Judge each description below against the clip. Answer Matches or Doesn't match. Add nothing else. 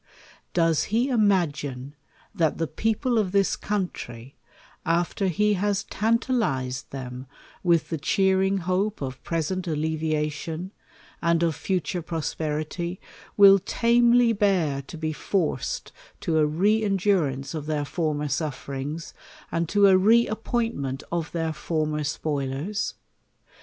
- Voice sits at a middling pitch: Matches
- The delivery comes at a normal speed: Doesn't match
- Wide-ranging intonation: Doesn't match